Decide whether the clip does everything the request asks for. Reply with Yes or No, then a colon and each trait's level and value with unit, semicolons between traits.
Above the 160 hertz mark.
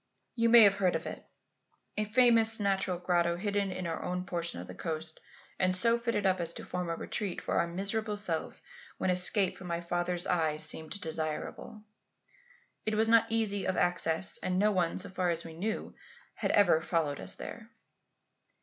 Yes: medium, 185 Hz